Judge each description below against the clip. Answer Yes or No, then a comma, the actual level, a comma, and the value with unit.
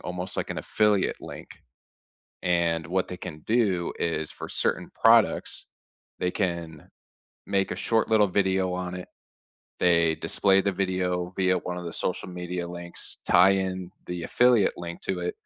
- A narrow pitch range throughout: Yes, narrow, 1.7 semitones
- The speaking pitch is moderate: No, very low, 90 Hz